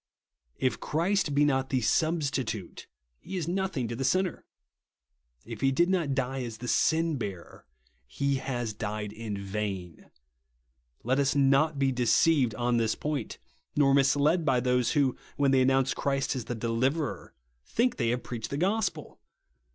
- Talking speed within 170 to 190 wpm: No, average, 160 wpm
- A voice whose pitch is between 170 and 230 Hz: No, low, 135 Hz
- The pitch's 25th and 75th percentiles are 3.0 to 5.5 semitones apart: Yes, average, 3.9 semitones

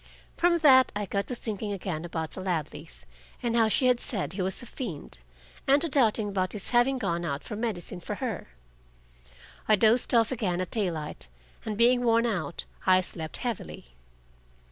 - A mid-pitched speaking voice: No, high, 210 Hz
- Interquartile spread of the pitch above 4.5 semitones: Yes, average, 5.2 semitones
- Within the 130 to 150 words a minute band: No, average, 180 wpm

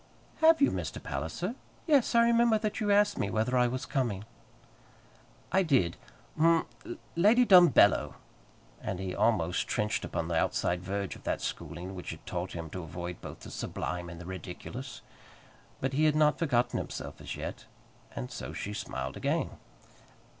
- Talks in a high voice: No, low, 120 Hz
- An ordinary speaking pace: Yes, average, 165 wpm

